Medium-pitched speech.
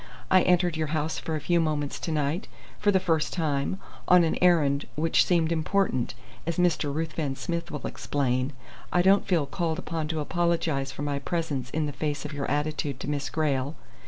Yes: medium, 155 Hz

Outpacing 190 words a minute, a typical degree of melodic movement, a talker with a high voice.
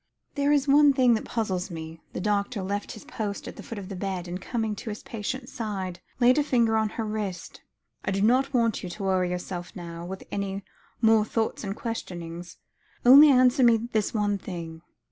Yes: average, 200 wpm; average, 4.1 semitones; high, 210 Hz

